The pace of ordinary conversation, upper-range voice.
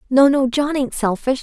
No: fast, 210 wpm; very high, 265 Hz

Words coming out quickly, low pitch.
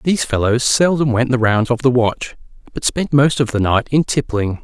Yes: fast, 220 wpm; low, 125 Hz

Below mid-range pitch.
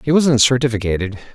Yes: low, 120 Hz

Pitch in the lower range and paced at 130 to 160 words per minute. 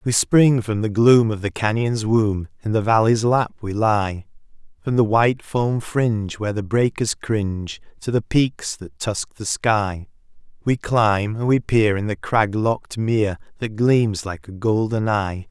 No: low, 110 Hz; average, 180 wpm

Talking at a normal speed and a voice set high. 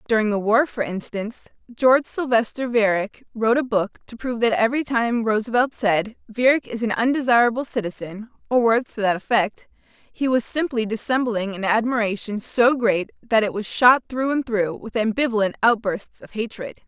Yes: average, 170 wpm; high, 230 Hz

